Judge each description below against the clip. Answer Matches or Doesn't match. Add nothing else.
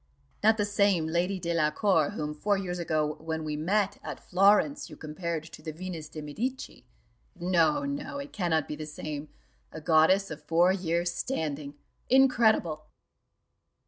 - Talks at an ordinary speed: Matches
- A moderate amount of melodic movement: Matches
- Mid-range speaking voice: Matches